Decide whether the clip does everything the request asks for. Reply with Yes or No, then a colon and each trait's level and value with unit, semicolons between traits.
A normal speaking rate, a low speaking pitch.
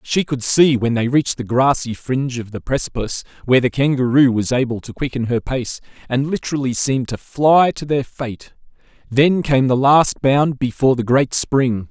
Yes: average, 190 wpm; low, 130 Hz